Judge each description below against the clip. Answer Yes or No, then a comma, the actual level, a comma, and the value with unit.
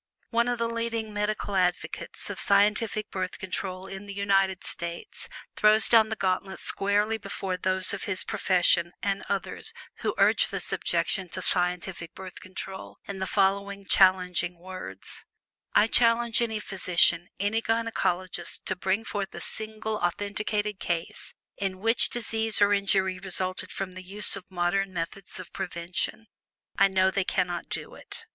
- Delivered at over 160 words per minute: No, average, 150 wpm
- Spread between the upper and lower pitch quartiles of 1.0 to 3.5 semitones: Yes, narrow, 2.4 semitones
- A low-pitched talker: No, high, 195 Hz